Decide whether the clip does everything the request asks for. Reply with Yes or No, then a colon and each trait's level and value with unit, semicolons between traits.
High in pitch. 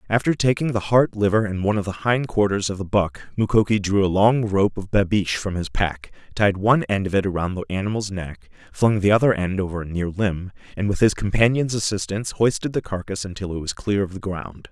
No: low, 100 Hz